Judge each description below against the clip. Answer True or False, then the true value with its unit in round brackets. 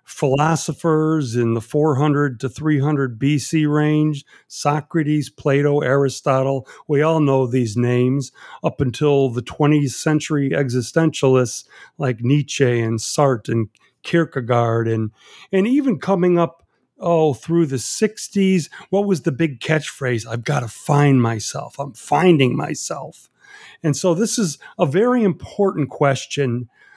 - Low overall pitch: False (145 Hz)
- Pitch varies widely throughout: False (3.5 semitones)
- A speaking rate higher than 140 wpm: False (135 wpm)